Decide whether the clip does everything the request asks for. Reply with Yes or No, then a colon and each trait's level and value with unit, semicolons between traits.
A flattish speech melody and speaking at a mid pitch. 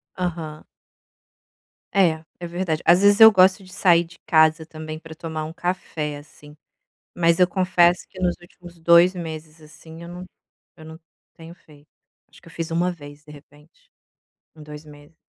Yes: narrow, 2.2 semitones; medium, 165 Hz